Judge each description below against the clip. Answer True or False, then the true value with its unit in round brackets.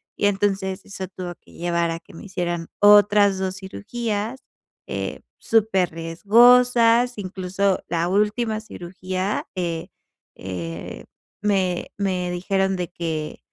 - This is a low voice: False (190 Hz)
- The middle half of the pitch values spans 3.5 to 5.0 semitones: False (2.8 semitones)